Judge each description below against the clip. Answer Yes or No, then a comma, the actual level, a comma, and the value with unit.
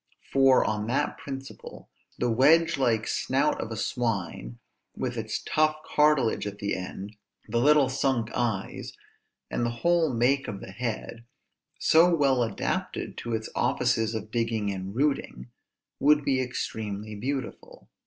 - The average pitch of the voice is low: Yes, low, 120 Hz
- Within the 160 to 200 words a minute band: No, average, 145 wpm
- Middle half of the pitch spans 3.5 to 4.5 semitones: Yes, average, 4.1 semitones